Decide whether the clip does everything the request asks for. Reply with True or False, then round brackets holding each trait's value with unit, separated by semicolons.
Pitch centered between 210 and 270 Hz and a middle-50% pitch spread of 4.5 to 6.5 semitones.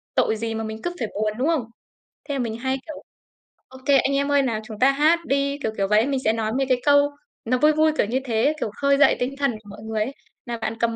False (255 Hz; 4.1 semitones)